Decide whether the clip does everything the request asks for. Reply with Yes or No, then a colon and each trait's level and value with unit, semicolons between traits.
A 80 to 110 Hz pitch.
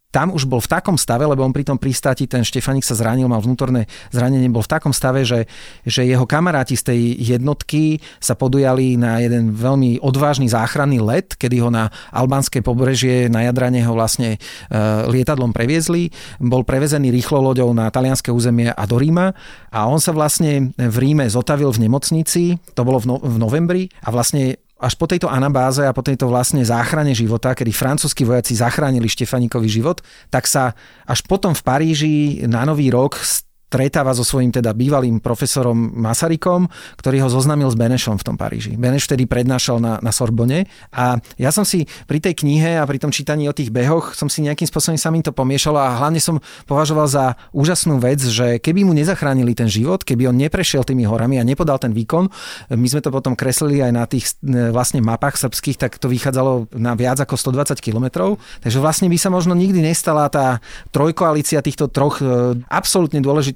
No: low, 130 Hz